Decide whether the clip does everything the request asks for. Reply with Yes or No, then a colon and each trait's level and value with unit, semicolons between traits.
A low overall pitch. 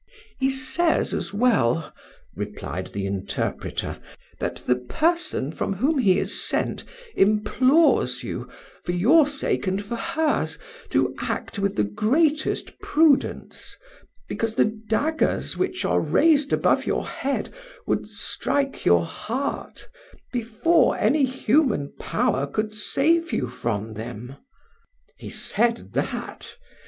No: high, 230 Hz